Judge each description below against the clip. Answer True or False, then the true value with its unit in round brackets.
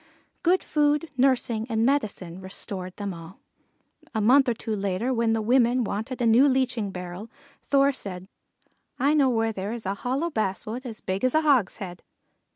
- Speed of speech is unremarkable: True (170 wpm)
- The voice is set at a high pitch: True (230 Hz)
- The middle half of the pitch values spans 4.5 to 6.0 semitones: True (4.9 semitones)